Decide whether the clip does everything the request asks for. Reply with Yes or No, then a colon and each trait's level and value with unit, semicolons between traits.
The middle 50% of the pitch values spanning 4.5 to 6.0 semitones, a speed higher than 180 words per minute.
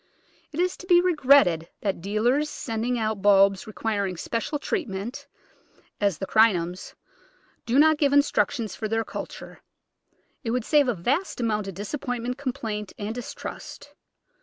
No: wide, 5.6 semitones; average, 155 wpm